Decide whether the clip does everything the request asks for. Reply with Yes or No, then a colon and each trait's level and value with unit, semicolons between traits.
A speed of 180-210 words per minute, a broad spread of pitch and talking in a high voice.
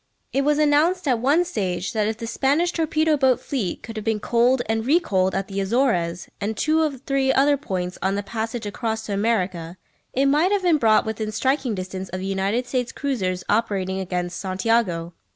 Yes: average, 200 wpm; wide, 6.2 semitones; high, 225 Hz